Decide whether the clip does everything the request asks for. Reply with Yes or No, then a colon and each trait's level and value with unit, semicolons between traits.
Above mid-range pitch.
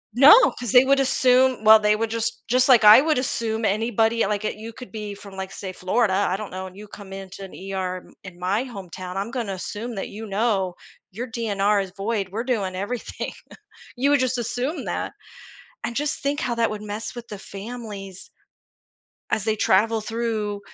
Yes: high, 215 Hz